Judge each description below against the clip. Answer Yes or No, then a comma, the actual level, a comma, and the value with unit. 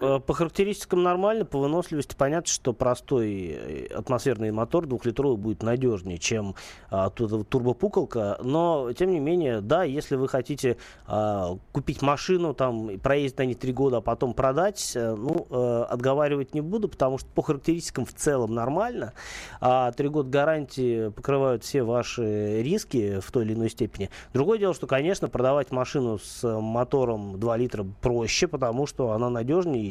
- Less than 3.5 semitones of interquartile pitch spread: No, average, 4.4 semitones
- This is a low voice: Yes, low, 130 Hz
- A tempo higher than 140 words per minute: Yes, average, 155 wpm